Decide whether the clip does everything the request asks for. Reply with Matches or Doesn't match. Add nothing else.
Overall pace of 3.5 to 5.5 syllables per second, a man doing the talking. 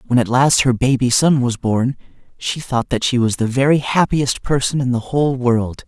Matches